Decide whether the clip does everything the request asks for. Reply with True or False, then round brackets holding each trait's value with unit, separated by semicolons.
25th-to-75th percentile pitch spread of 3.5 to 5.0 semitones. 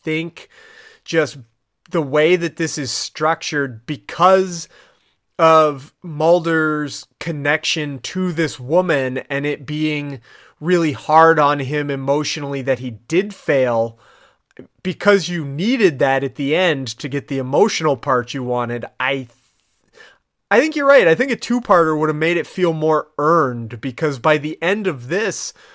True (3.8 semitones)